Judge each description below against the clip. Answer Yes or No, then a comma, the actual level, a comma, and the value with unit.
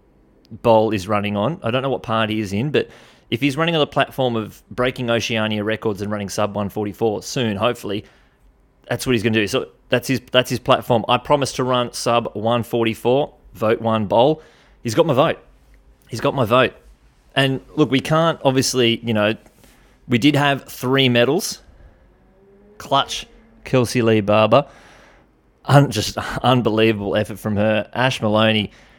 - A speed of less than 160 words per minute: No, average, 170 wpm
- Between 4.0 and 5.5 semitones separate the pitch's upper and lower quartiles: No, average, 3.5 semitones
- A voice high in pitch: No, low, 115 Hz